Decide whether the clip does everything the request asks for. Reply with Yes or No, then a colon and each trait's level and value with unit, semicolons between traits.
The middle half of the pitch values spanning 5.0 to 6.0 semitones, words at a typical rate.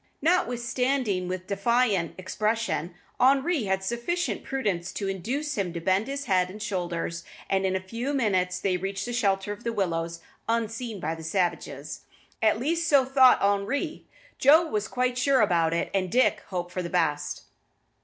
Yes: wide, 5.5 semitones; average, 170 wpm